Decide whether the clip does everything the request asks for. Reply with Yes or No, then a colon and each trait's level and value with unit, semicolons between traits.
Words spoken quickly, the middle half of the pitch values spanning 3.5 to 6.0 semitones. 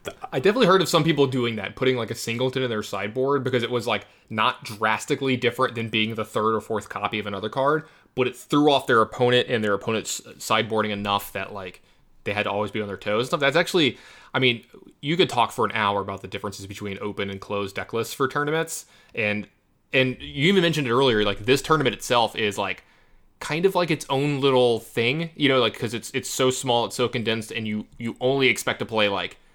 Yes: fast, 235 wpm; average, 4.2 semitones